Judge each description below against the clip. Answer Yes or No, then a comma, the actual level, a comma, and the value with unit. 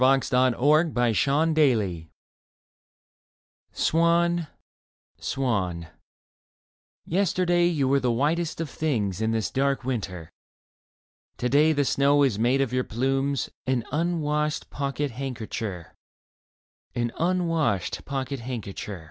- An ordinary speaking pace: No, slow, 115 wpm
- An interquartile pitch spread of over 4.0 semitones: Yes, average, 4.6 semitones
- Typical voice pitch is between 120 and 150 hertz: Yes, low, 135 Hz